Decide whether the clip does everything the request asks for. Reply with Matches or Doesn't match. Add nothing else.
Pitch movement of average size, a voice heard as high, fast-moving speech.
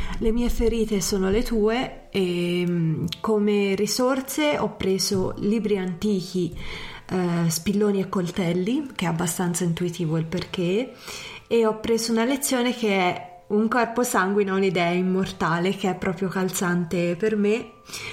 Doesn't match